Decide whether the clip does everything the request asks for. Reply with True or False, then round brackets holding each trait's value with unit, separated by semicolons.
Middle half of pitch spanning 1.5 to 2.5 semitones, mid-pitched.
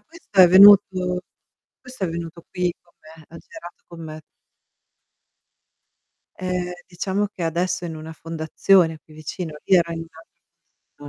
True (2.2 semitones; 175 Hz)